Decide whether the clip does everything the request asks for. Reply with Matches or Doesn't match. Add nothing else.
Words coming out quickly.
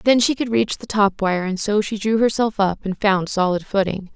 Matches